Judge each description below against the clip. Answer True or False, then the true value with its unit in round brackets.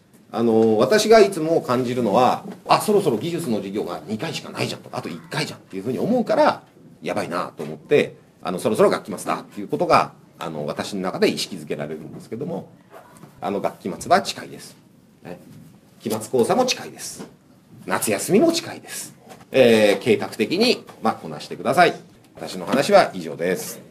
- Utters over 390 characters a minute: False (365 characters per minute)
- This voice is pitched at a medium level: True (165 Hz)